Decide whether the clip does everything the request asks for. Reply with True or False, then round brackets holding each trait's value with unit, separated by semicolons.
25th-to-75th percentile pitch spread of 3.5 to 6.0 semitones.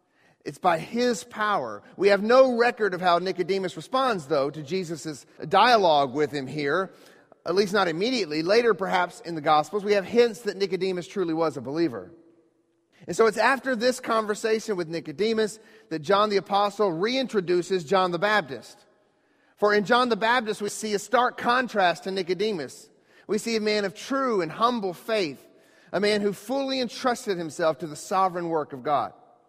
True (4.5 semitones)